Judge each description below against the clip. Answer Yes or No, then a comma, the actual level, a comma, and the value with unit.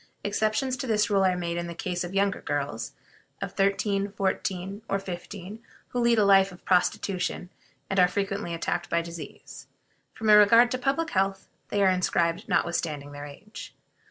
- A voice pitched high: Yes, high, 195 Hz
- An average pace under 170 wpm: No, average, 175 wpm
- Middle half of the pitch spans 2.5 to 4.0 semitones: Yes, average, 3.0 semitones